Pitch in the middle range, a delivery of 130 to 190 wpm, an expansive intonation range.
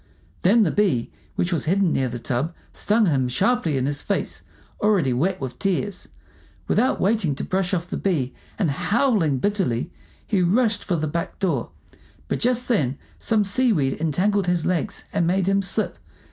Yes: medium, 180 Hz; average, 175 wpm; wide, 5.9 semitones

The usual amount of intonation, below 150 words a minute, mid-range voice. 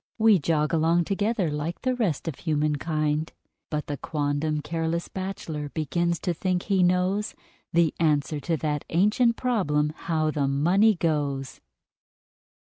Yes: average, 3.5 semitones; average, 140 wpm; medium, 165 Hz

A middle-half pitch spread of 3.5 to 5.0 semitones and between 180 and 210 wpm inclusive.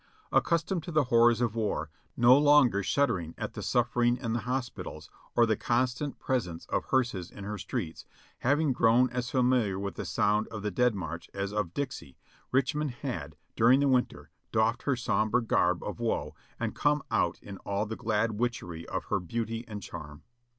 Yes: average, 3.8 semitones; average, 185 wpm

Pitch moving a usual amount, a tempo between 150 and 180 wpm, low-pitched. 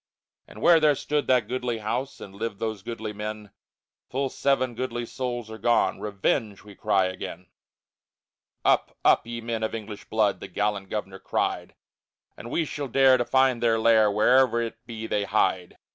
Yes: average, 3.1 semitones; average, 175 wpm; low, 115 Hz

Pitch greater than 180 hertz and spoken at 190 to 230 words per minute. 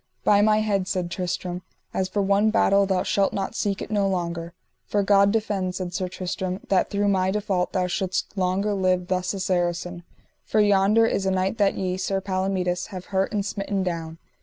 Yes: high, 190 Hz; average, 195 wpm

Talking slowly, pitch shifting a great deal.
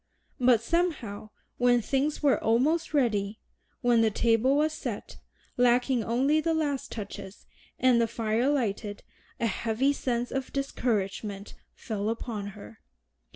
No: slow, 130 wpm; average, 4.0 semitones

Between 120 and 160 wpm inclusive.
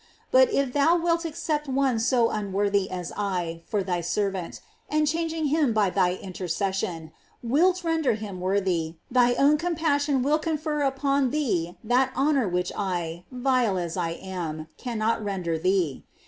Yes: average, 155 wpm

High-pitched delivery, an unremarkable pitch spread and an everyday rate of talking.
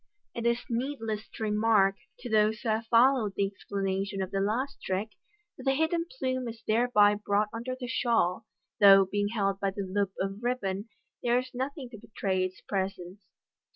Yes: high, 215 Hz; average, 3.5 semitones; average, 185 wpm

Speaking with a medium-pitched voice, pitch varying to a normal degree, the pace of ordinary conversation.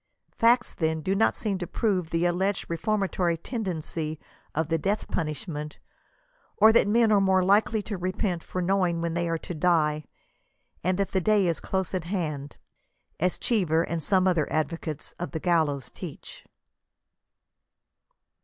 Yes: medium, 180 Hz; average, 3.4 semitones; average, 160 wpm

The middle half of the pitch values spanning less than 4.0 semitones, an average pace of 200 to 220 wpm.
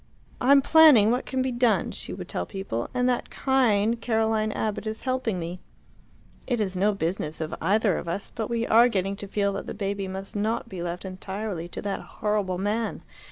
Yes: average, 3.4 semitones; fast, 205 wpm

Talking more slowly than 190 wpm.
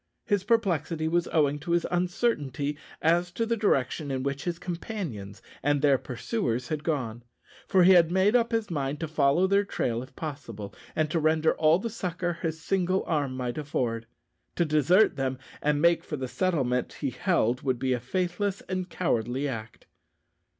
Yes: average, 175 wpm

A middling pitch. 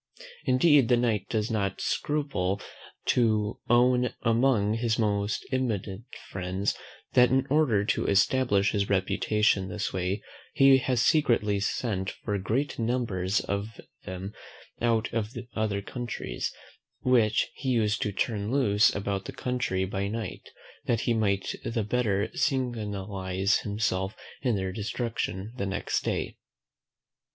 No: low, 110 Hz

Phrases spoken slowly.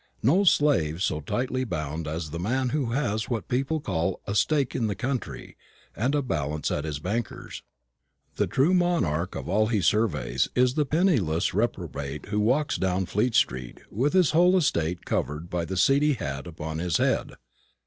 No: average, 175 wpm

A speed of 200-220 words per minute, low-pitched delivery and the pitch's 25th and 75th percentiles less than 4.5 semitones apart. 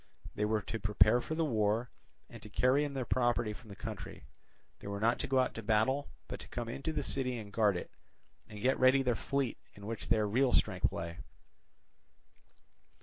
Yes: fast, 205 wpm; low, 115 Hz; average, 3.5 semitones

